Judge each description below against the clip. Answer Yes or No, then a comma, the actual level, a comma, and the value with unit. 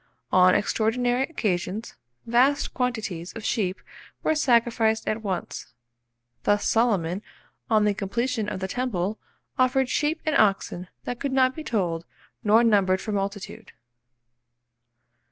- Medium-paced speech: No, slow, 125 wpm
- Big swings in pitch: No, average, 4.2 semitones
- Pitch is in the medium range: No, high, 220 Hz